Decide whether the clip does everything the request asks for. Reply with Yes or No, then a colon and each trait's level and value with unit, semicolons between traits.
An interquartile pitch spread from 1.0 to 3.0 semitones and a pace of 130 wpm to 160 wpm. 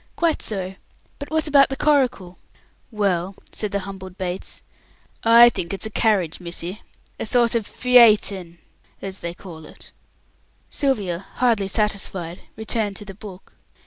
No: average, 4.0 semitones; average, 140 wpm